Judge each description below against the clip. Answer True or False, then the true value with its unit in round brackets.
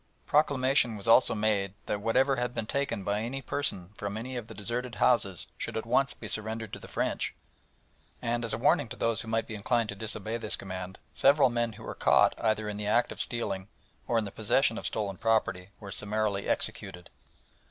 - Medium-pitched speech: False (110 Hz)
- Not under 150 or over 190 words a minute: False (205 wpm)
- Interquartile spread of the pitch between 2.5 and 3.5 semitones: True (2.8 semitones)